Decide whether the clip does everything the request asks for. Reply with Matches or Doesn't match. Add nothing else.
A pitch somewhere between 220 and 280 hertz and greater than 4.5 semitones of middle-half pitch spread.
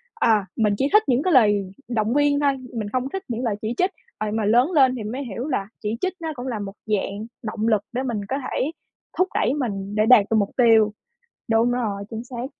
Doesn't match